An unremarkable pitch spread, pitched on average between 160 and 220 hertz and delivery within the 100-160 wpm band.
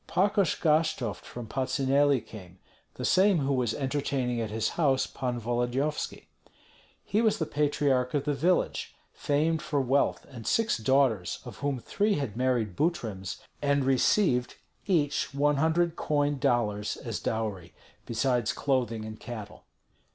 No: average, 4.0 semitones; low, 135 Hz; average, 140 wpm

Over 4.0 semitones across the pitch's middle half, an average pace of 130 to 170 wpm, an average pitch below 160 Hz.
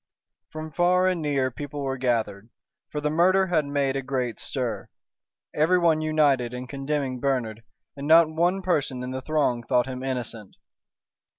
No: average, 3.7 semitones; average, 160 wpm; medium, 140 Hz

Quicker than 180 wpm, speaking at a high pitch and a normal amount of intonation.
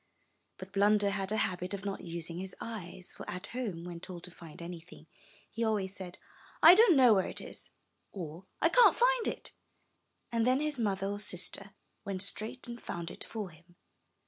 Yes: average, 190 wpm; high, 195 Hz; average, 4.1 semitones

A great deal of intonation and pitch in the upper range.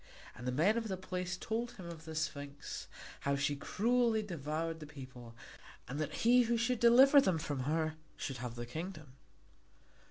No: wide, 7.5 semitones; medium, 160 Hz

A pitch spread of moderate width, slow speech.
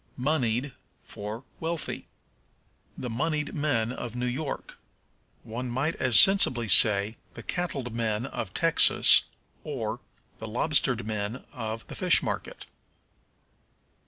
Yes: average, 4.5 semitones; slow, 115 wpm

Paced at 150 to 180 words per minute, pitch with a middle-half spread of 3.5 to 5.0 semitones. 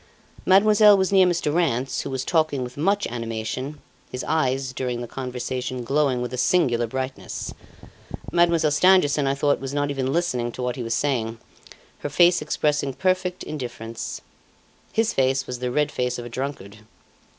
Yes: average, 165 wpm; average, 4.3 semitones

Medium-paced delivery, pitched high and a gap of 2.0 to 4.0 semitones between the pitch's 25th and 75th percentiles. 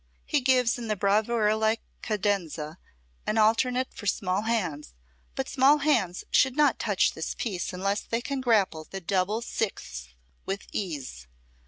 No: average, 150 wpm; high, 210 Hz; average, 4.4 semitones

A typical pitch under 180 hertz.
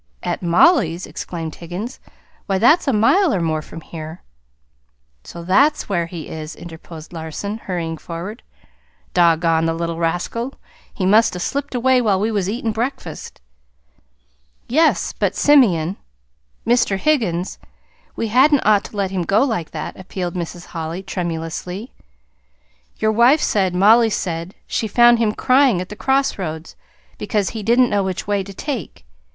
No: high, 195 Hz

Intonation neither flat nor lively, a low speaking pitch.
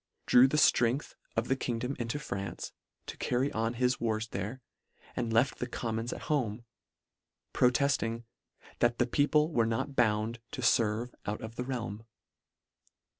No: narrow, 2.3 semitones; low, 120 Hz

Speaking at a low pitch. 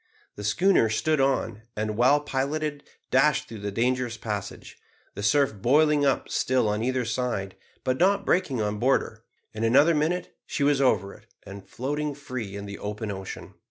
Yes: low, 125 Hz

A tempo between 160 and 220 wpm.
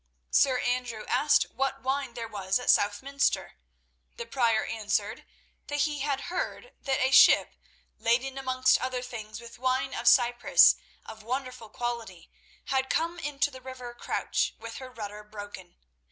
No: average, 150 wpm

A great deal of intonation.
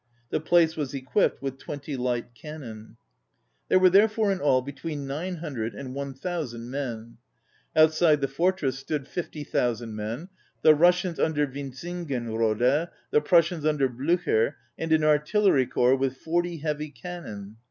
No: average, 4.7 semitones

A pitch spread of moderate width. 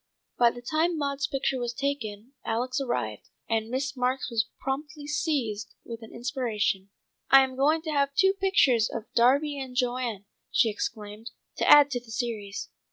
Yes: average, 3.8 semitones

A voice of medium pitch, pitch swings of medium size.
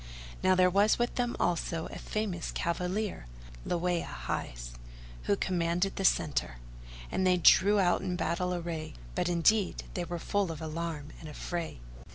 No: medium, 175 Hz; narrow, 2.2 semitones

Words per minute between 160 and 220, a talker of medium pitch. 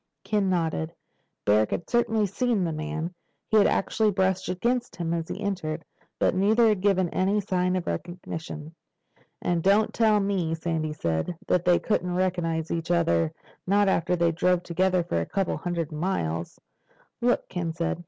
Yes: average, 165 wpm; medium, 180 Hz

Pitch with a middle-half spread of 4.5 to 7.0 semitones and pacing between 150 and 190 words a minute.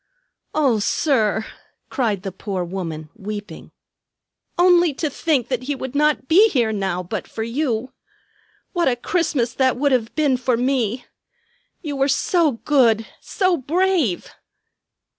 No: wide, 5.5 semitones; average, 140 wpm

